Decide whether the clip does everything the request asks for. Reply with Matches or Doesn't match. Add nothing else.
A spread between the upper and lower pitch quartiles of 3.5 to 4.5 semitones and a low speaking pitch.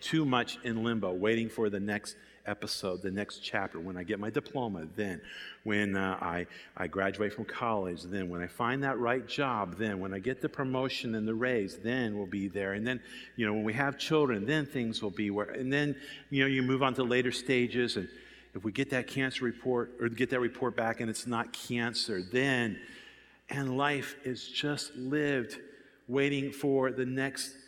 Matches